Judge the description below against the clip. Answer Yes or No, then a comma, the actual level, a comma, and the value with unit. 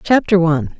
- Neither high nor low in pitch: Yes, medium, 175 Hz